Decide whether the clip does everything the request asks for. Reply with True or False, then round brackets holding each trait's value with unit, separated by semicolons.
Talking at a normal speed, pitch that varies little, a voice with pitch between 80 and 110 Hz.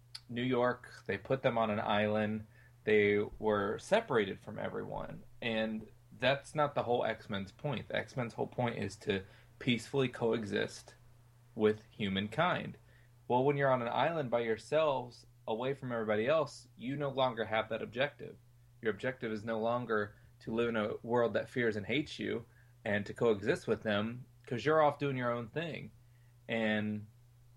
False (170 wpm; 2.3 semitones; 120 Hz)